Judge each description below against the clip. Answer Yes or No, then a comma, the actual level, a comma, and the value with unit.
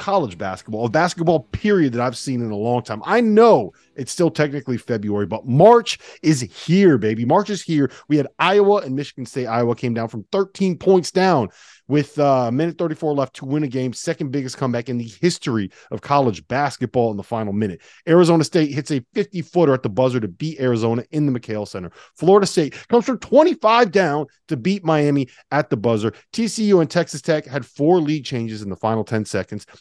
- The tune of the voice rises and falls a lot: Yes, wide, 6.5 semitones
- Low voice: No, medium, 145 Hz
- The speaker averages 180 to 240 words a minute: Yes, fast, 205 wpm